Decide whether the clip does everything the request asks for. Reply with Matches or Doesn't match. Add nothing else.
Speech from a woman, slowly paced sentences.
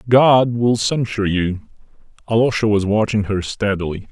Doesn't match